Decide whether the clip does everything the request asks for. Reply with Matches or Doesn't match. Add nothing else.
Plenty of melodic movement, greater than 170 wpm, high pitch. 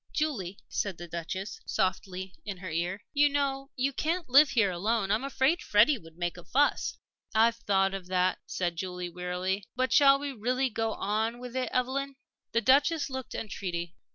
Matches